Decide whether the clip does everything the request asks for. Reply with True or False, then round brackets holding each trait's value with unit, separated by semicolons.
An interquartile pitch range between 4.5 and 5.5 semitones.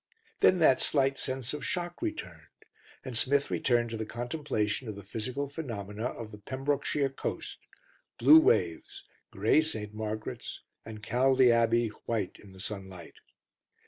True (4.8 semitones)